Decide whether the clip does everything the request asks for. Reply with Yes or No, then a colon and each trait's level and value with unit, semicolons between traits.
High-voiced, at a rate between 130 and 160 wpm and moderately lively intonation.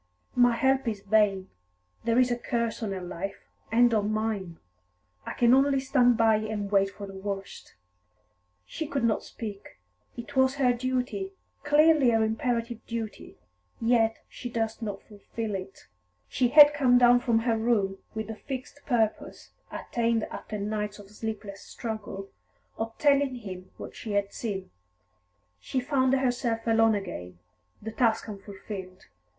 Yes: high, 225 Hz; average, 150 wpm; average, 3.3 semitones